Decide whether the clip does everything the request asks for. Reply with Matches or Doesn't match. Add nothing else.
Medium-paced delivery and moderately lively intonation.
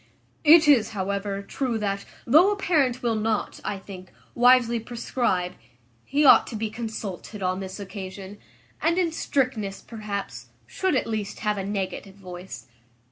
Matches